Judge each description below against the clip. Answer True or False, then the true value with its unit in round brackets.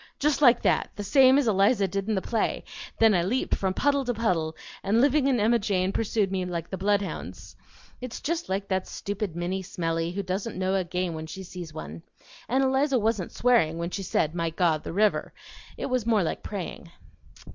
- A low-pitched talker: False (195 Hz)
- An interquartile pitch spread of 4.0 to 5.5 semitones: True (4.7 semitones)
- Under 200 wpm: False (205 wpm)